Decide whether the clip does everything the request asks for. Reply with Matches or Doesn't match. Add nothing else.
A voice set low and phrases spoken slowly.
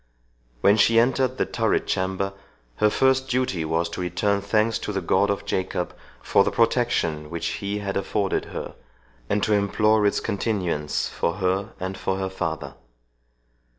Doesn't match